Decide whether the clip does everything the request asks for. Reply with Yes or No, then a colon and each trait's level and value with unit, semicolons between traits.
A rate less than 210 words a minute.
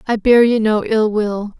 No: fast, 225 wpm